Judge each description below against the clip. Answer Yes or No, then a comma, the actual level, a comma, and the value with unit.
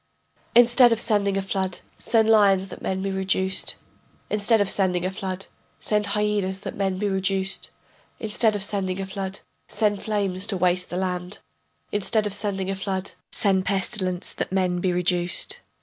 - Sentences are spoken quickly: No, average, 165 wpm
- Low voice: No, high, 195 Hz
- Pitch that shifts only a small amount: Yes, narrow, 1.7 semitones